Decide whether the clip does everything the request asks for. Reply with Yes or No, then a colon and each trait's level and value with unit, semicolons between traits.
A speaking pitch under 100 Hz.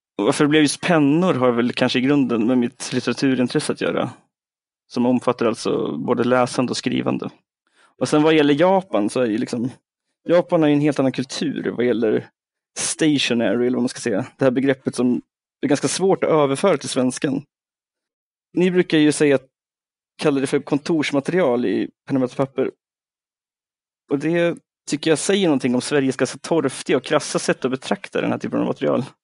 No: medium, 140 Hz